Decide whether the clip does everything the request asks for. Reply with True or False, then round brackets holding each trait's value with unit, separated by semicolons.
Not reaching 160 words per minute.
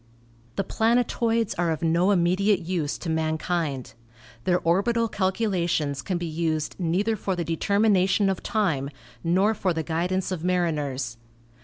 True (145 wpm)